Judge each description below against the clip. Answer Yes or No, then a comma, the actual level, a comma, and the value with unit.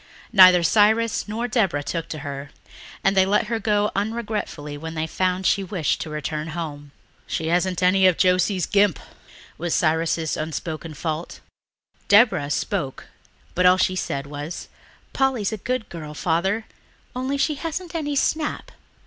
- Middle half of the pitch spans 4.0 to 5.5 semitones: Yes, average, 5.1 semitones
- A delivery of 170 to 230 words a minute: No, average, 160 wpm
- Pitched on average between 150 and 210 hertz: Yes, medium, 185 Hz